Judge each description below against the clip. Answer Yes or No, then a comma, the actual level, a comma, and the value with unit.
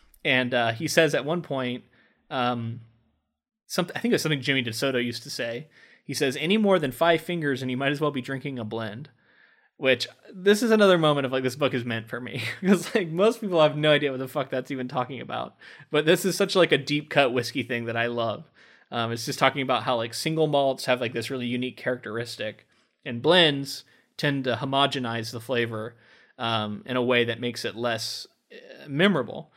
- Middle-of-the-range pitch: No, low, 130 Hz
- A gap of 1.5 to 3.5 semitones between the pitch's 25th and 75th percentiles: No, average, 3.9 semitones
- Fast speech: Yes, fast, 215 wpm